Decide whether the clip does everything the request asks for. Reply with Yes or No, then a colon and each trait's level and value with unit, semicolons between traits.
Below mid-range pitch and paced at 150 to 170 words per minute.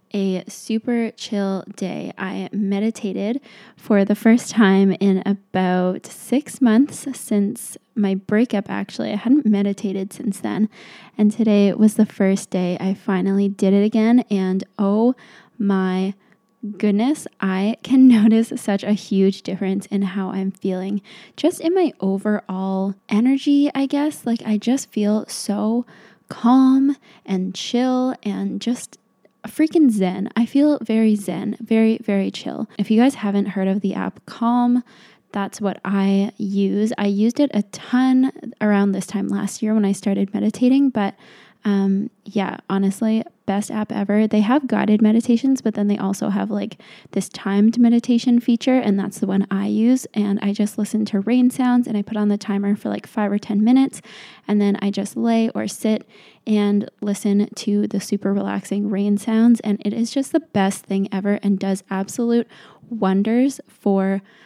No: high, 210 Hz; average, 165 wpm